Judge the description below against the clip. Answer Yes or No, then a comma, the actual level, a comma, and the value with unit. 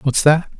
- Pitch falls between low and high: Yes, medium, 145 Hz